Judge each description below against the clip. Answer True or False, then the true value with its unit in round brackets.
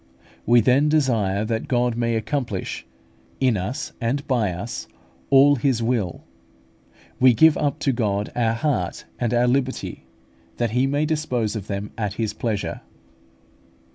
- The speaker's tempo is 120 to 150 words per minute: True (145 wpm)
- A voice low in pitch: True (120 Hz)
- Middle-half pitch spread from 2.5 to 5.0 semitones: True (3.7 semitones)